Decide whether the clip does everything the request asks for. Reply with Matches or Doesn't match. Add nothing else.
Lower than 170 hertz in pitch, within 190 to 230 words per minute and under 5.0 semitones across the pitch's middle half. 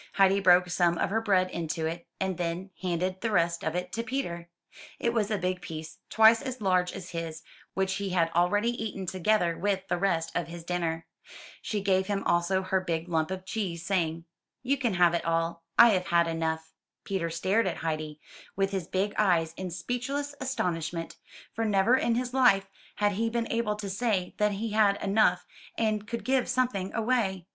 Doesn't match